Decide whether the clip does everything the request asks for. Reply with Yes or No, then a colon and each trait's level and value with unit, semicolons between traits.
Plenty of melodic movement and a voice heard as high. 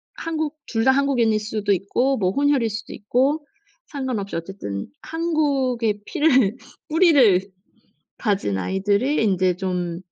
Yes: wide, 6.3 semitones; high, 225 Hz